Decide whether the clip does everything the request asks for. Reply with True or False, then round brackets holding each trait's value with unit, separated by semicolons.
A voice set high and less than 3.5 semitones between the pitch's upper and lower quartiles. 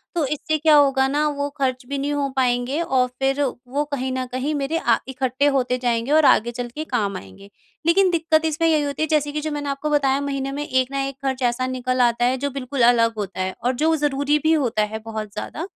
True (270 Hz; 2.8 semitones)